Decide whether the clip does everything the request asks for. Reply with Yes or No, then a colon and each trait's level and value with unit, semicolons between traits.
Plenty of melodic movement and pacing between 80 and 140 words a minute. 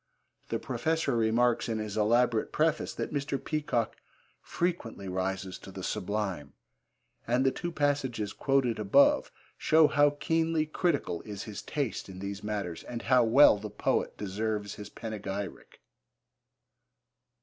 Yes: wide, 5.8 semitones; slow, 135 wpm